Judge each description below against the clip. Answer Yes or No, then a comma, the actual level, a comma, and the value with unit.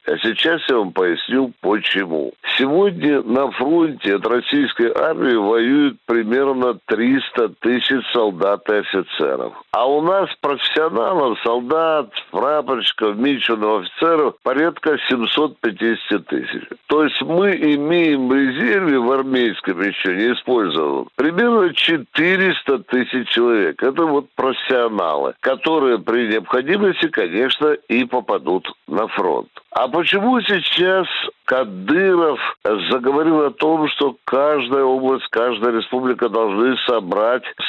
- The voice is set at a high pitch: No, low, 135 Hz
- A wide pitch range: Yes, wide, 6.2 semitones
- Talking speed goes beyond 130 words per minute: No, slow, 110 wpm